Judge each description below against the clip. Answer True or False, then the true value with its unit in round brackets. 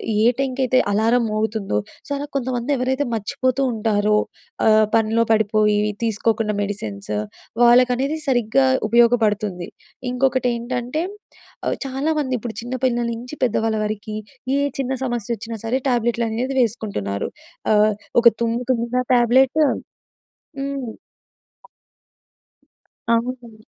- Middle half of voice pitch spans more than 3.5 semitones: False (2.8 semitones)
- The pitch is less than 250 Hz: True (235 Hz)